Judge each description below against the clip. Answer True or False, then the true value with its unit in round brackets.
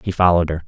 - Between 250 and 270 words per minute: True (265 wpm)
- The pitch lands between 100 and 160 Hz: False (85 Hz)